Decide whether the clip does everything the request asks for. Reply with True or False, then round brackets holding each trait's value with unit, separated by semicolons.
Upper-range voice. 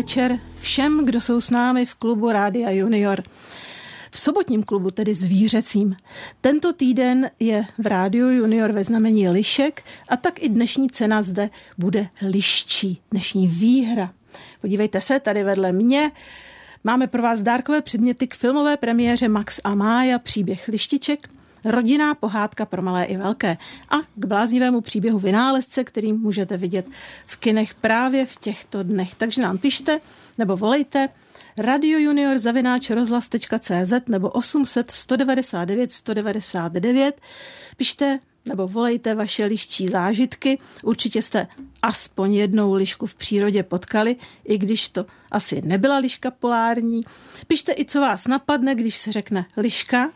True (225 Hz)